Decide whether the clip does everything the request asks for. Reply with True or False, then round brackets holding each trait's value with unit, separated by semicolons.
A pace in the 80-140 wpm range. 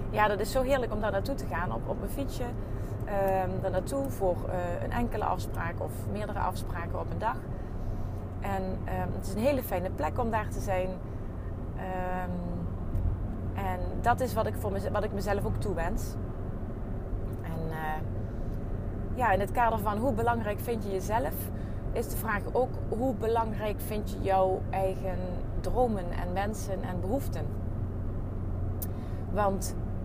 False (160 wpm)